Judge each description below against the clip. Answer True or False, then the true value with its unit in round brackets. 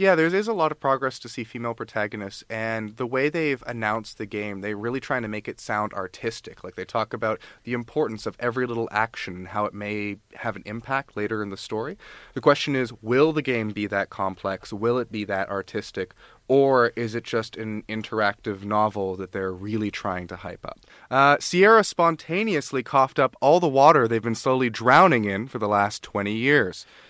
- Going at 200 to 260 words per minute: True (205 wpm)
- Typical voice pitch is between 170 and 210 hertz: False (115 Hz)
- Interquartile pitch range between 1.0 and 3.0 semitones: False (4.0 semitones)